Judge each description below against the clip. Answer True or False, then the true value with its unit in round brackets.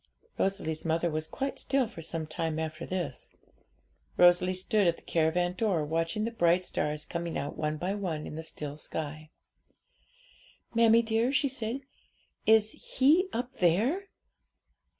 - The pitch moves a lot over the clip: True (5.8 semitones)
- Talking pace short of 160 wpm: True (150 wpm)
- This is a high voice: False (175 Hz)